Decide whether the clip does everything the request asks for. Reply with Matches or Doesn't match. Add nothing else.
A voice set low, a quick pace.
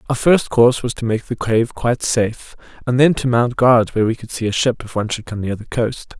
Matches